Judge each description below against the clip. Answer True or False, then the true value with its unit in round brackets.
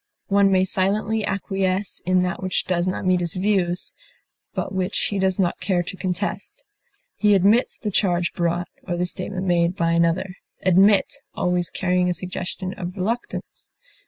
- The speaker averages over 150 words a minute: True (160 wpm)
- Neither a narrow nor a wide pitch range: False (1.7 semitones)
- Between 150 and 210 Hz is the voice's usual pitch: True (185 Hz)